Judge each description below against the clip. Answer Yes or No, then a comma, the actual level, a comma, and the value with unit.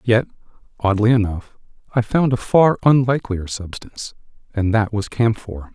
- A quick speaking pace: No, slow, 135 wpm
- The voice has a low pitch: Yes, low, 110 Hz